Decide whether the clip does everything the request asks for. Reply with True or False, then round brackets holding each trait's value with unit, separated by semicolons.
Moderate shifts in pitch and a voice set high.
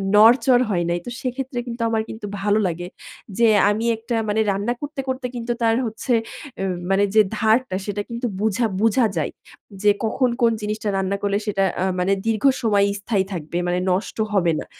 True (3.2 semitones; 220 Hz)